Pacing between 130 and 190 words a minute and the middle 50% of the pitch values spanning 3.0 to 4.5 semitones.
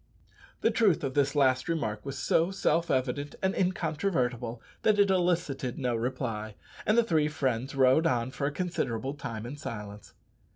No: average, 165 wpm; average, 5.2 semitones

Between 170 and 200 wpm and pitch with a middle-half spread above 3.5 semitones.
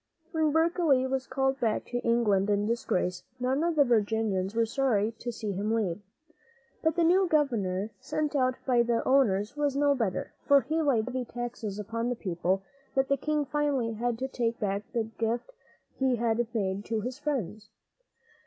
Yes: average, 180 wpm; average, 4.3 semitones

